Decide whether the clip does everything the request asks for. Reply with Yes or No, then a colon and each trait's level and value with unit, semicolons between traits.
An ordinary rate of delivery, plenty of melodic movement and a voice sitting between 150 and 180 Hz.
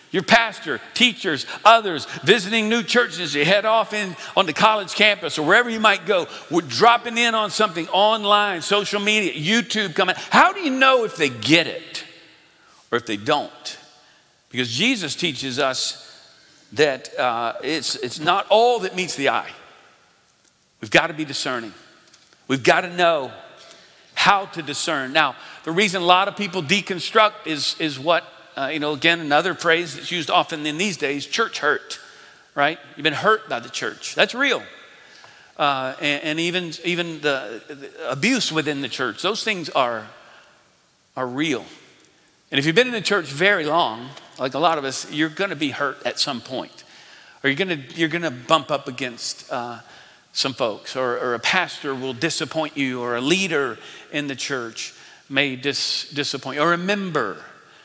Yes: average, 175 wpm; wide, 6.3 semitones; medium, 165 Hz